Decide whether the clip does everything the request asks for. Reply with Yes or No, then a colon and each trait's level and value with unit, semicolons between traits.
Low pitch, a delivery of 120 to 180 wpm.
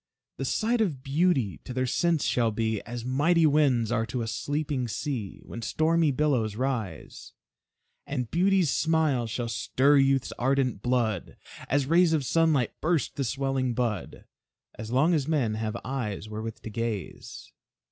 Yes: low, 130 Hz; average, 155 wpm